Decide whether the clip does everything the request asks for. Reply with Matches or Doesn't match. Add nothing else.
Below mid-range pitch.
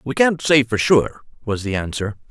Matches